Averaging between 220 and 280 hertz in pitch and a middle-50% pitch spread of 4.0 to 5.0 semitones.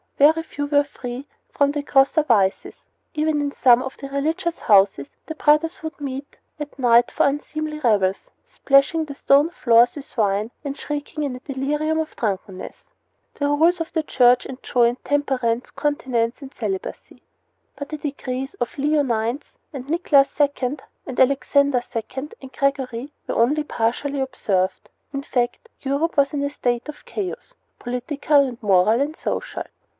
No: very high, 275 Hz; average, 3.4 semitones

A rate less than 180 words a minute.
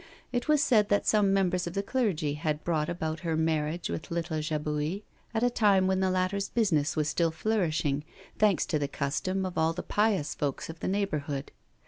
No: average, 195 wpm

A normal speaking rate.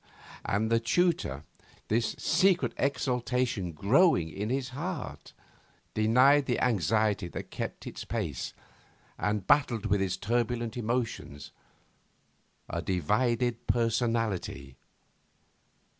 No: slow, 100 wpm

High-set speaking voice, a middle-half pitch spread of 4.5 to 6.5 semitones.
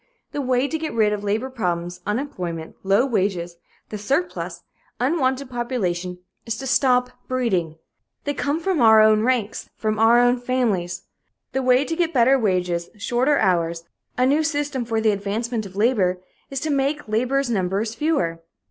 Yes: high, 235 Hz; average, 5.1 semitones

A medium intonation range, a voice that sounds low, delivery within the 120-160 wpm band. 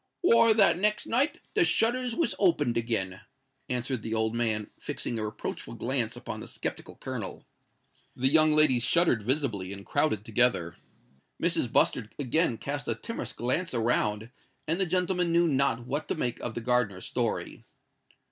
No: wide, 7.1 semitones; low, 130 Hz; average, 155 wpm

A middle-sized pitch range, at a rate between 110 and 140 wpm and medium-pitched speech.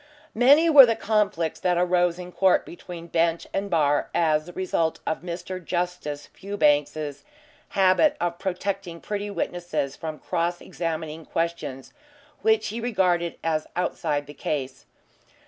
Yes: average, 3.1 semitones; slow, 135 wpm; medium, 175 Hz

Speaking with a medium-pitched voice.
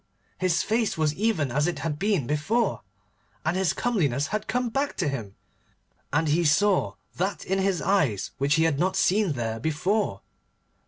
Yes: medium, 175 Hz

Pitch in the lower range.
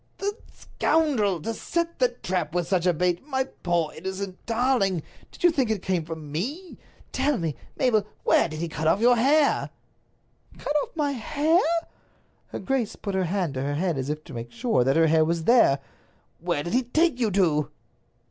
No: high, 195 Hz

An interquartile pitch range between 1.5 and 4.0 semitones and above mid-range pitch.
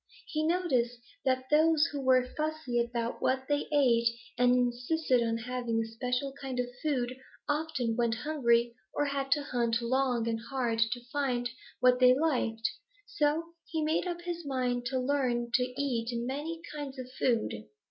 Yes: average, 3.4 semitones; very high, 255 Hz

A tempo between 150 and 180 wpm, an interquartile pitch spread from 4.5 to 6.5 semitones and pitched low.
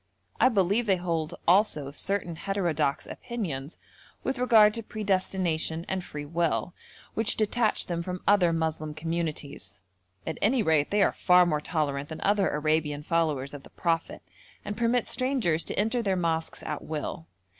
No: average, 155 wpm; average, 4.8 semitones; medium, 170 Hz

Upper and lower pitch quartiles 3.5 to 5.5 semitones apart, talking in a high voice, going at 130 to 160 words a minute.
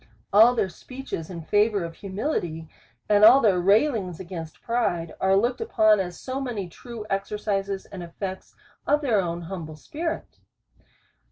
Yes: average, 4.8 semitones; high, 200 Hz; average, 150 wpm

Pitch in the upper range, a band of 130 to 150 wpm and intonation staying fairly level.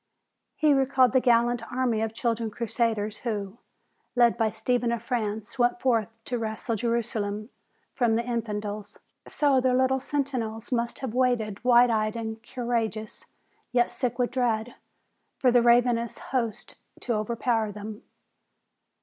Yes: high, 235 Hz; average, 140 wpm; narrow, 2.1 semitones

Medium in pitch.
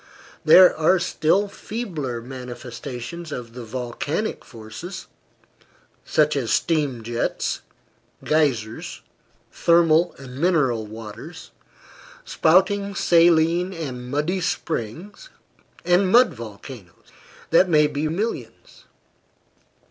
Yes: medium, 155 Hz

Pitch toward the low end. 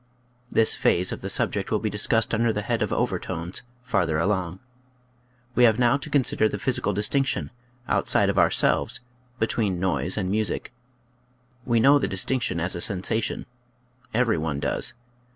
Yes: low, 110 Hz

